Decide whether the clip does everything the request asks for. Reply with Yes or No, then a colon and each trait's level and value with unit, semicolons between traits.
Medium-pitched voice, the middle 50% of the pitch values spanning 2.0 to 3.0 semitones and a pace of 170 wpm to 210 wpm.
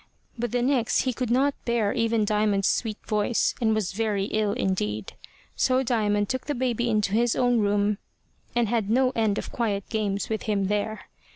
No: high, 220 Hz; average, 2.7 semitones; average, 185 wpm